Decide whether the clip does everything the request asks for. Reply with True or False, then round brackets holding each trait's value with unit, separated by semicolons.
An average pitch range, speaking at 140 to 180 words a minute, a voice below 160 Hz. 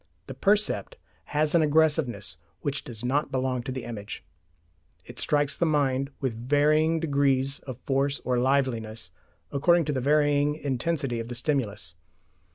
True (3.2 semitones; 150 wpm; 140 Hz)